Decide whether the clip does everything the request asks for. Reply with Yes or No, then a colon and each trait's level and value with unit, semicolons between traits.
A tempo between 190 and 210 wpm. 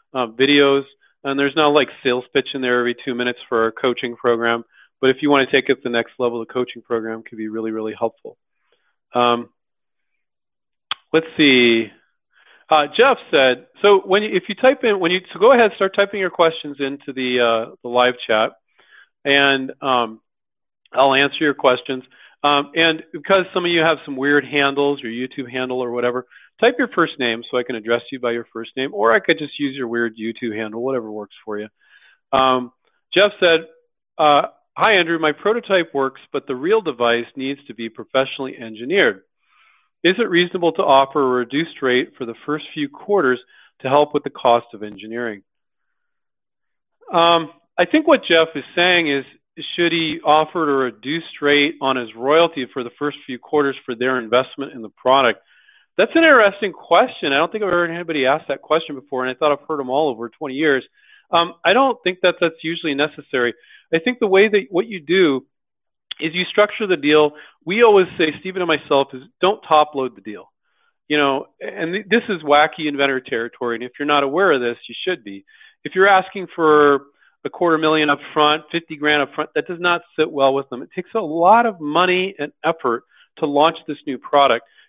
Yes: average, 200 wpm